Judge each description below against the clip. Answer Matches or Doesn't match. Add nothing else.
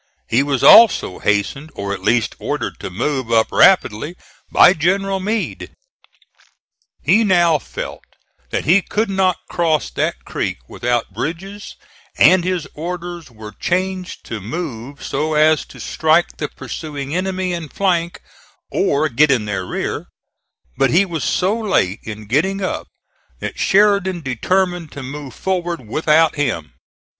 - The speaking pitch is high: Doesn't match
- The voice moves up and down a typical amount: Doesn't match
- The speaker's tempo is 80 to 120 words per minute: Doesn't match